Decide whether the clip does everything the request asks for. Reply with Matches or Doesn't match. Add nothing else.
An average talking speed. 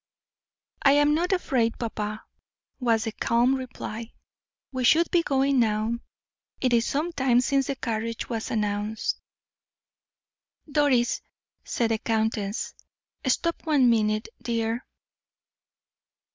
Doesn't match